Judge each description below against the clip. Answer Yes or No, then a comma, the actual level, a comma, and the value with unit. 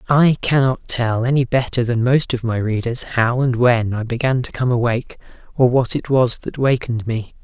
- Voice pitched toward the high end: No, low, 125 Hz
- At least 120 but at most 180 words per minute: No, average, 200 wpm